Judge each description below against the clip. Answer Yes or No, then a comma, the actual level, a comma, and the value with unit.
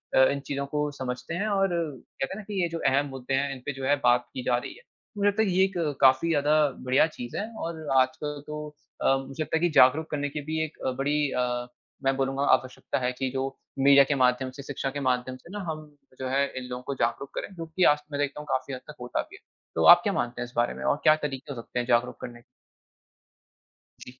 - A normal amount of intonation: Yes, average, 3.2 semitones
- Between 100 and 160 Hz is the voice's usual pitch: Yes, medium, 140 Hz